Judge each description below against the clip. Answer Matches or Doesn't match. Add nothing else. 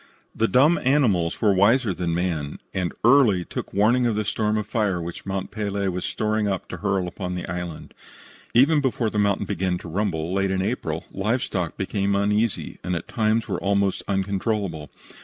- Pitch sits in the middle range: Doesn't match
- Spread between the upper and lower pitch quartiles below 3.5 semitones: Matches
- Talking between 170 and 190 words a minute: Matches